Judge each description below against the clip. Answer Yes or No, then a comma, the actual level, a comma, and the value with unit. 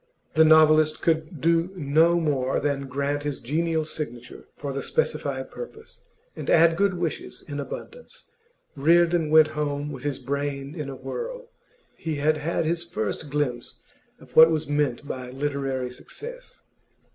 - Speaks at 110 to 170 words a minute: Yes, average, 150 wpm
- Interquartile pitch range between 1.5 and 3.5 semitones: Yes, average, 3.0 semitones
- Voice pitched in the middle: Yes, medium, 150 Hz